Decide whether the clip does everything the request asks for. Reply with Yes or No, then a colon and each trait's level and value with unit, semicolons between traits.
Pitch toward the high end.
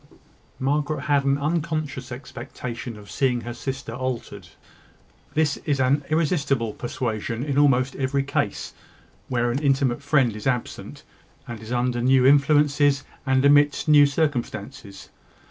No: low, 135 Hz